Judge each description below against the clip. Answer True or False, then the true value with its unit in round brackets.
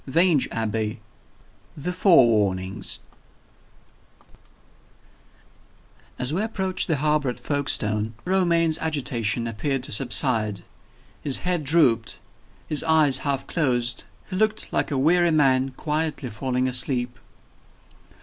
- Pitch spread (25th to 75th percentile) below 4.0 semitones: False (5.2 semitones)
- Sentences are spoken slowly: True (110 wpm)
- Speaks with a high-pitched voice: False (135 Hz)